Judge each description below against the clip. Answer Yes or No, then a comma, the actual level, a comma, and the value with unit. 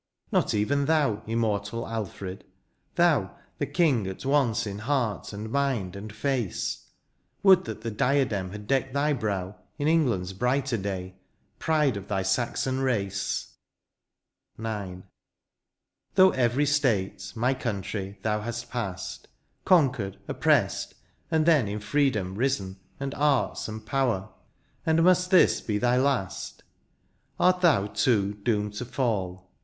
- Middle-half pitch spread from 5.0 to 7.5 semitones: Yes, wide, 5.6 semitones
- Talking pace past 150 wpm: No, slow, 135 wpm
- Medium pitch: No, low, 115 Hz